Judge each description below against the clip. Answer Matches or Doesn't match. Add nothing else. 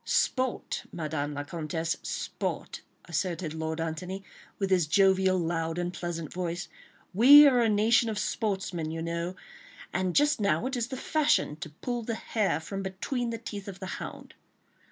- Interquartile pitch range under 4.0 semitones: Doesn't match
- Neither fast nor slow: Matches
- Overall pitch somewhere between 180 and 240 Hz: Matches